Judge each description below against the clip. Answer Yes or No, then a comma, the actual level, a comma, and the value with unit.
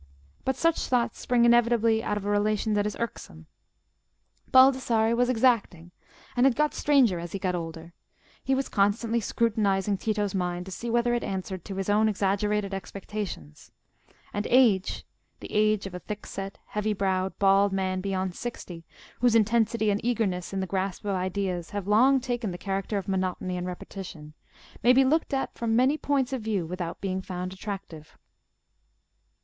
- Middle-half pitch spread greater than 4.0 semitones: No, average, 3.7 semitones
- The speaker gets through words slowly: No, average, 165 wpm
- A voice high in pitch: Yes, high, 205 Hz